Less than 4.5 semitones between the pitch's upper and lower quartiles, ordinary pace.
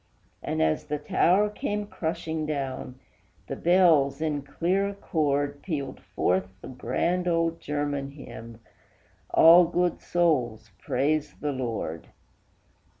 No: average, 4.1 semitones; slow, 115 wpm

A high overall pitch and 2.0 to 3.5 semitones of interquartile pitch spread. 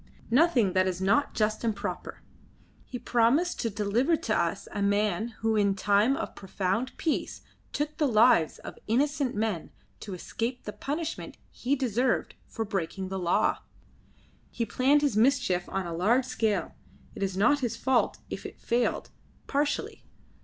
No: high, 225 Hz; average, 4.8 semitones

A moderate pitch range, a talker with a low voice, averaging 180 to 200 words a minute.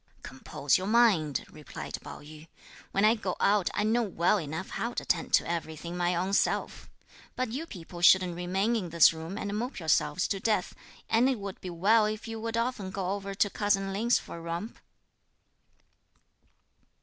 No: average, 4.2 semitones; high, 195 Hz; average, 185 wpm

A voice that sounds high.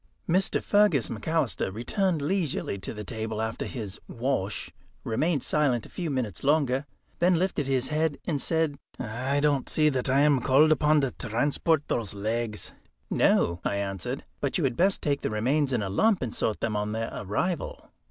No: low, 135 Hz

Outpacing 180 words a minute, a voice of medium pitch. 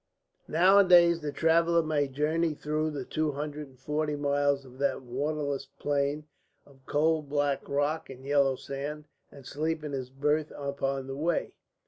No: average, 155 wpm; medium, 145 Hz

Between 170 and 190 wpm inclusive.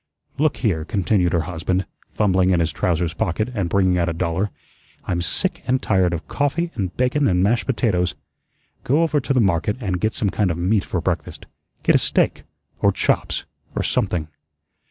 Yes: average, 185 wpm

